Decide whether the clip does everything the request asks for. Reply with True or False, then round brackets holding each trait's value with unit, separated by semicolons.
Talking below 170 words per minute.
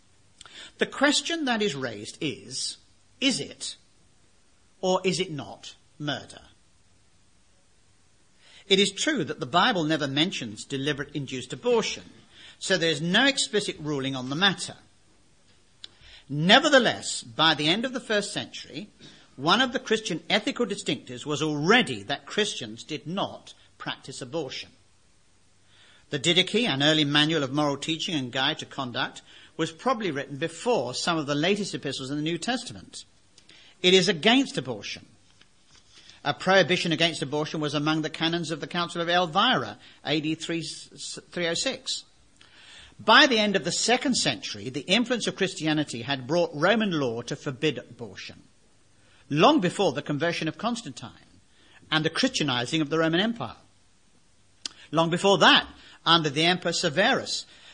True (140 wpm)